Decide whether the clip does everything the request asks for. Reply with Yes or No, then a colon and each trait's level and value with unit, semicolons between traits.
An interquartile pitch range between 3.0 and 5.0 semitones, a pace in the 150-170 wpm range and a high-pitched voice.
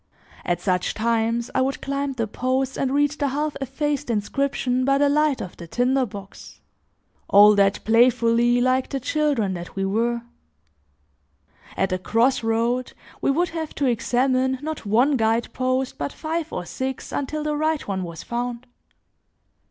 Yes: average, 3.8 semitones; average, 160 wpm; very high, 250 Hz